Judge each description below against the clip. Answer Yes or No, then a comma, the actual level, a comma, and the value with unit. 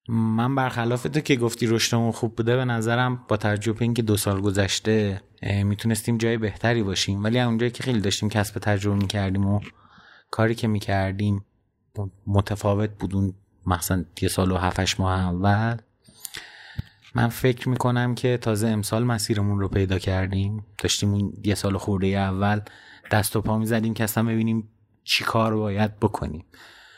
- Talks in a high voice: No, low, 105 Hz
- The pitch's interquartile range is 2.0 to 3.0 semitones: Yes, narrow, 2.6 semitones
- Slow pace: No, fast, 155 wpm